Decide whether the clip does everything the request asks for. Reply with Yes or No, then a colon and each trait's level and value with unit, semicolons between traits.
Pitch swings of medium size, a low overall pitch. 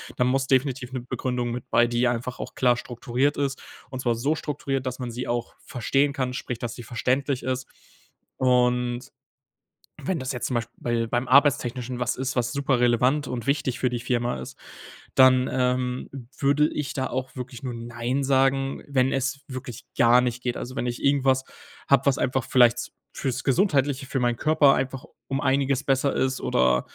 No: narrow, 1.8 semitones; low, 130 Hz